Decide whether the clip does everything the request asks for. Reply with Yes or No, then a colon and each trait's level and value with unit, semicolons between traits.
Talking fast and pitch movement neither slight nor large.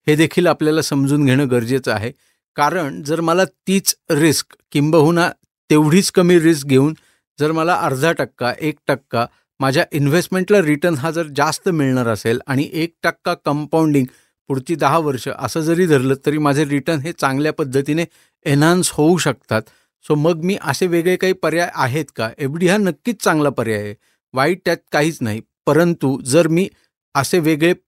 Yes: fast, 160 wpm; average, 3.6 semitones